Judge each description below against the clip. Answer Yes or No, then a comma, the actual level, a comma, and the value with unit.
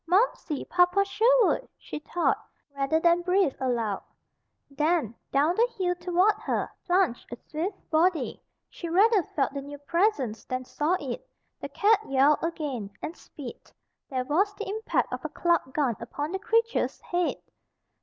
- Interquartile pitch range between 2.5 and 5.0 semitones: No, wide, 5.6 semitones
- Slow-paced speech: No, average, 155 wpm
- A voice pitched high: Yes, very high, 335 Hz